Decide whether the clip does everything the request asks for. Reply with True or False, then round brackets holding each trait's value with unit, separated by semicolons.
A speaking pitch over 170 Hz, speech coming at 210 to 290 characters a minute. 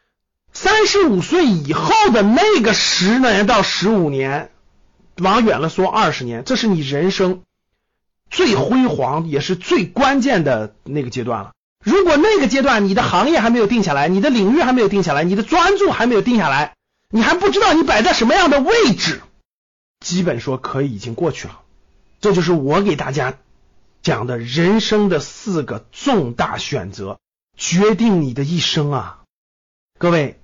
True (190 Hz; 250 characters per minute)